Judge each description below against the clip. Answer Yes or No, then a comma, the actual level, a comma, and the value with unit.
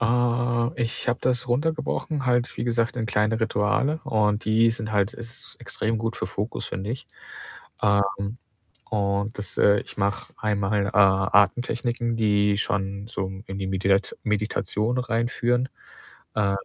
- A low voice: Yes, low, 110 Hz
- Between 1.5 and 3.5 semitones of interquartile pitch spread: Yes, average, 2.9 semitones